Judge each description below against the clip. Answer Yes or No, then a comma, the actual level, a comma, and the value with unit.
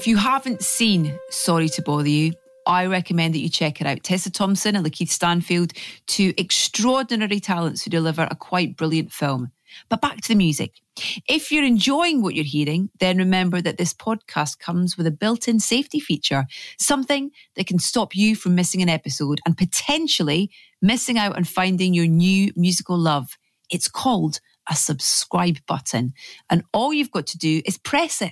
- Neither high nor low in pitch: Yes, medium, 180 Hz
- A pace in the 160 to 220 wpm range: Yes, average, 180 wpm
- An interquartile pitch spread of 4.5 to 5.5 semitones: Yes, average, 5.1 semitones